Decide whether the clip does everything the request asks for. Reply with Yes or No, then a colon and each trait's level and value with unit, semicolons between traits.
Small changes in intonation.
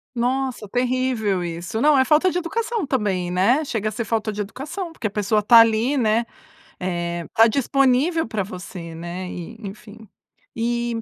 No: average, 5.0 semitones